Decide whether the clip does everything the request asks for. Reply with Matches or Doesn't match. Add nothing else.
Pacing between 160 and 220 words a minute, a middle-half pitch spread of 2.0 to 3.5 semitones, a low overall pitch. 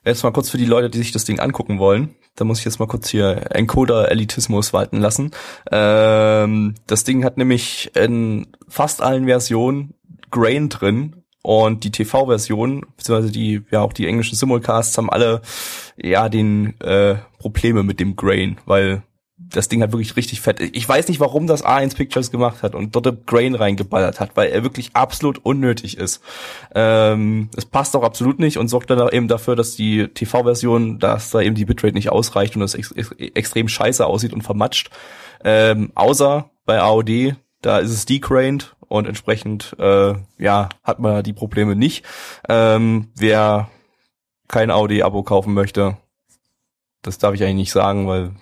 Matches